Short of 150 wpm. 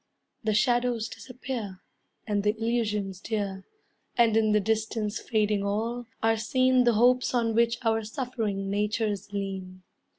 Yes: slow, 135 wpm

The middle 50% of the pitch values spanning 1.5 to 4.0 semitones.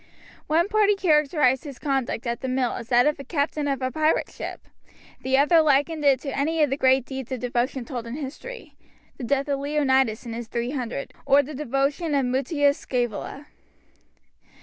Yes: average, 2.8 semitones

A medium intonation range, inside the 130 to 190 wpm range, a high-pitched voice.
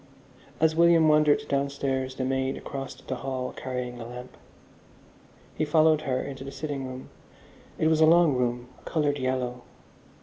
No: average, 3.0 semitones; average, 155 wpm; low, 135 Hz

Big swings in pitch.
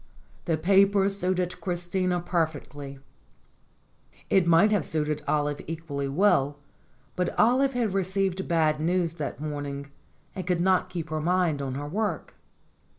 No: average, 4.0 semitones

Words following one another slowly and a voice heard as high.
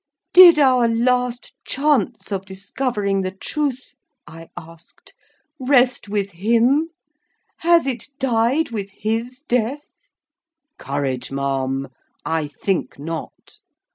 Yes: slow, 105 wpm; high, 225 Hz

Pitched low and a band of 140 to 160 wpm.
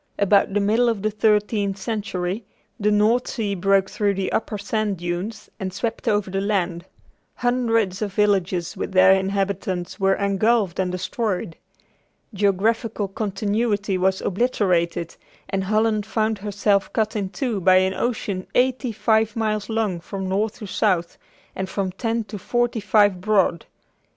No: high, 200 Hz; average, 150 wpm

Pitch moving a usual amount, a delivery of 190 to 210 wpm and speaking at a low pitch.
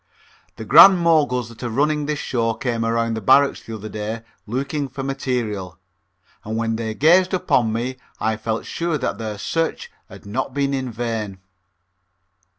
No: average, 4.0 semitones; average, 165 wpm; low, 120 Hz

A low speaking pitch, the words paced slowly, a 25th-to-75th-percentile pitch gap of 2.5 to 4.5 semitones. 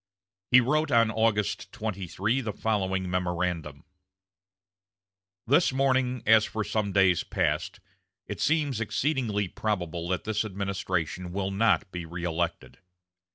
Yes: low, 100 Hz; slow, 115 wpm; average, 3.9 semitones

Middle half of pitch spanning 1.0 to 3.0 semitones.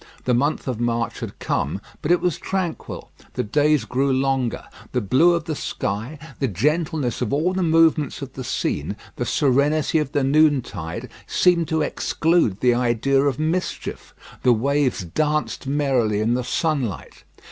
No: average, 4.2 semitones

